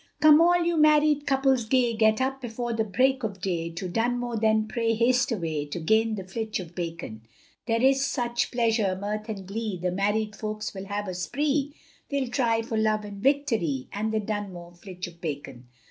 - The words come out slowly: No, average, 190 wpm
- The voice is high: Yes, high, 220 Hz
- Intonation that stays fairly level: No, average, 4.5 semitones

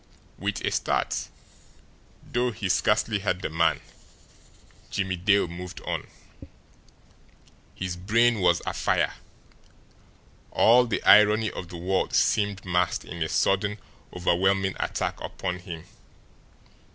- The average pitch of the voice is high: No, very low, 95 Hz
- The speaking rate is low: Yes, slow, 115 wpm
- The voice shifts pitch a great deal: No, average, 2.9 semitones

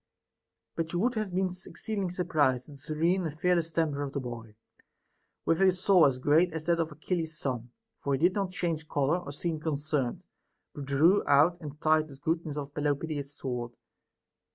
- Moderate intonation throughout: Yes, average, 3.5 semitones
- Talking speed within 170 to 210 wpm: Yes, average, 190 wpm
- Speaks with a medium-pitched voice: Yes, medium, 155 Hz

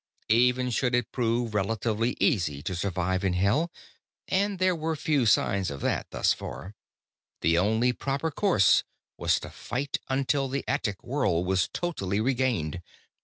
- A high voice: No, low, 120 Hz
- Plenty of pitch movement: Yes, wide, 6.2 semitones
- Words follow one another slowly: No, average, 150 wpm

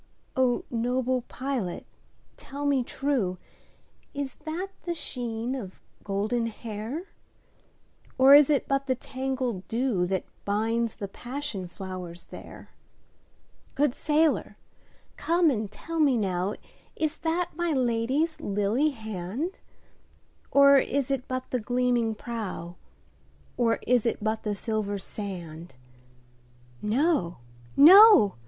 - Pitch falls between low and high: No, high, 240 Hz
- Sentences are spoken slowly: Yes, slow, 100 wpm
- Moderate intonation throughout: No, wide, 5.7 semitones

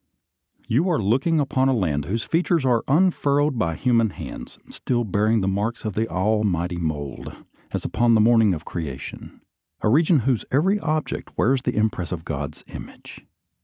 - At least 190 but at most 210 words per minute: No, average, 170 wpm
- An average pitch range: No, wide, 6.5 semitones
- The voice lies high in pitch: No, low, 115 Hz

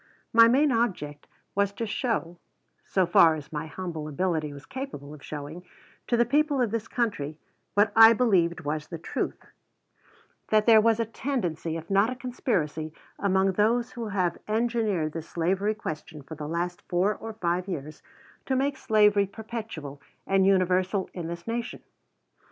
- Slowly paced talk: No, average, 165 wpm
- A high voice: Yes, high, 195 Hz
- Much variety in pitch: Yes, wide, 5.8 semitones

